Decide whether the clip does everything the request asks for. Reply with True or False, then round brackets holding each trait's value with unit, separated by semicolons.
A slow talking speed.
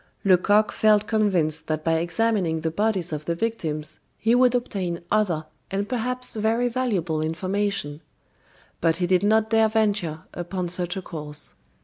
False (150 wpm)